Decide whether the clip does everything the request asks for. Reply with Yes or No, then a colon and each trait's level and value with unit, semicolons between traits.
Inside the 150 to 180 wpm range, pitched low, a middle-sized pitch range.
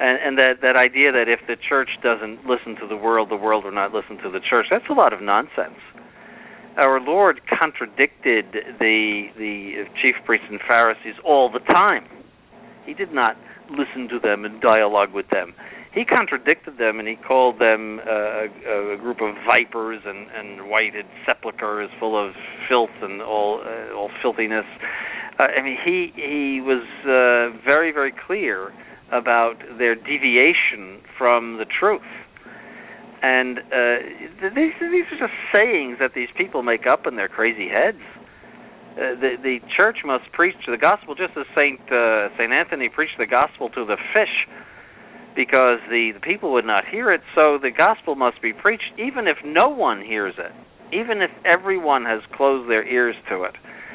Yes: average, 170 wpm; low, 120 Hz; average, 3.4 semitones